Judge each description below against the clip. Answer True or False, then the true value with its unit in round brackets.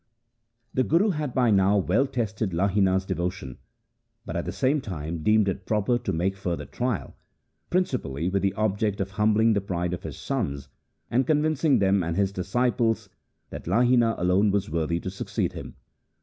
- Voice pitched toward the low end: True (100 Hz)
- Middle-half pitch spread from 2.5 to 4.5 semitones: False (4.9 semitones)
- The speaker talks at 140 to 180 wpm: True (170 wpm)